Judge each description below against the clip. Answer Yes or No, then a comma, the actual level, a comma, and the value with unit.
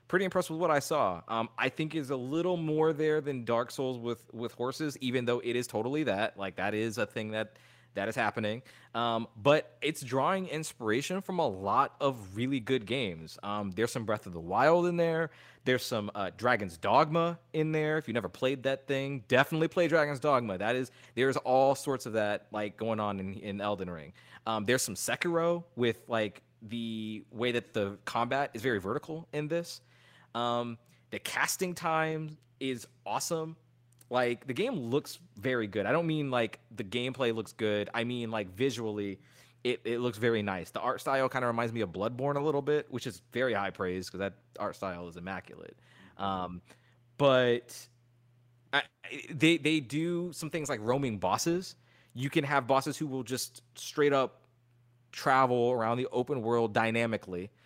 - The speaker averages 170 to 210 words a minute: Yes, average, 190 wpm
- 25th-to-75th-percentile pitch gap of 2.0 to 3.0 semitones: No, average, 4.3 semitones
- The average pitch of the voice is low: Yes, low, 125 Hz